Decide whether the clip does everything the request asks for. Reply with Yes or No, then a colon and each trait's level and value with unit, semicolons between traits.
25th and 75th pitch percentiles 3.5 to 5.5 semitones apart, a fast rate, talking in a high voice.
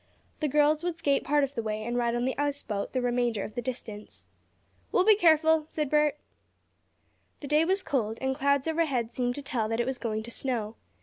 Yes: average, 4.2 semitones; fast, 220 wpm; very high, 265 Hz